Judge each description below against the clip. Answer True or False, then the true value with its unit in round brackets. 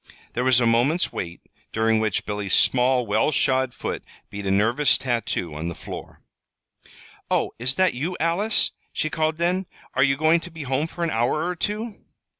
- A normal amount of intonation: False (6.6 semitones)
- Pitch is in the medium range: False (130 Hz)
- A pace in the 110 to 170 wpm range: False (185 wpm)